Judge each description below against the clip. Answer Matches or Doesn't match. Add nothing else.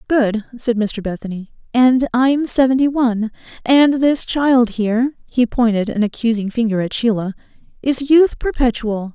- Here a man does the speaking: Doesn't match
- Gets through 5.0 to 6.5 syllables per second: Doesn't match